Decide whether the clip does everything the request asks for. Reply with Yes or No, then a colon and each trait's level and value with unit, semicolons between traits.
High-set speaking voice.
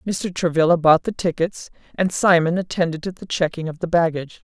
No: medium, 170 Hz